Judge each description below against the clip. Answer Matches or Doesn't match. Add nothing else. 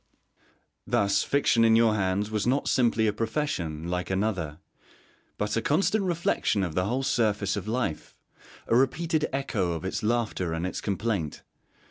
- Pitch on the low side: Matches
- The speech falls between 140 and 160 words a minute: Matches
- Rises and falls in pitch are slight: Doesn't match